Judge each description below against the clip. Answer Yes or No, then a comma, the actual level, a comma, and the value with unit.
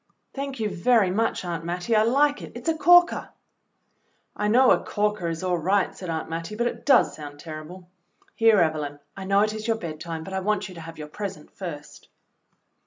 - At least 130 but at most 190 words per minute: No, fast, 205 wpm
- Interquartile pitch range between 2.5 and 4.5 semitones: No, average, 5.2 semitones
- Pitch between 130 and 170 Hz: No, high, 190 Hz